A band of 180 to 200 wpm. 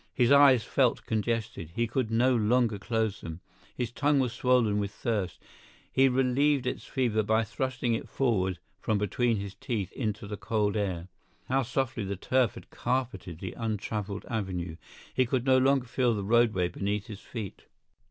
No: average, 165 wpm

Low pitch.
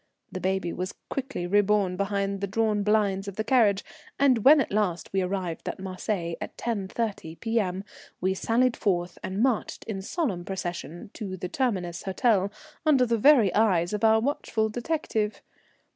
No: high, 200 Hz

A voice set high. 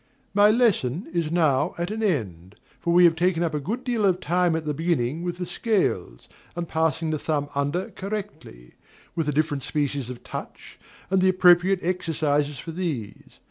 No: medium, 165 Hz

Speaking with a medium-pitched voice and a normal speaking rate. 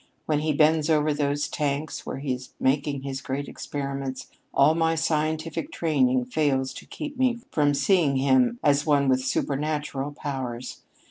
Yes: medium, 145 Hz; average, 160 wpm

